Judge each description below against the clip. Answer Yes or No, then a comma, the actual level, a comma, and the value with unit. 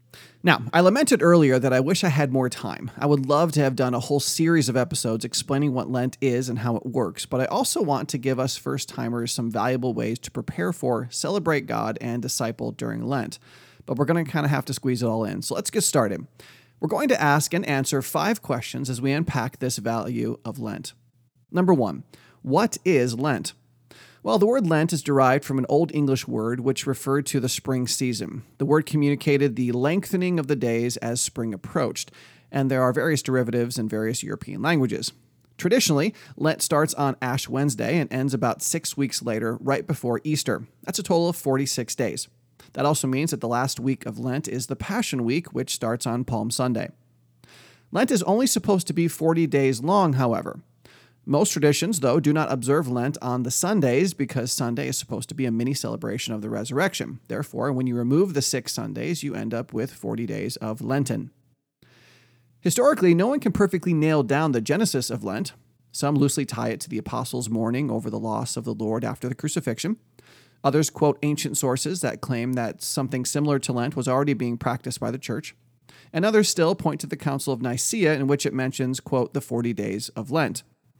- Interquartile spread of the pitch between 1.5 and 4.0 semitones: Yes, average, 3.5 semitones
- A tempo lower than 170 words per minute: No, fast, 205 wpm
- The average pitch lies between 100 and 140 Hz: Yes, low, 135 Hz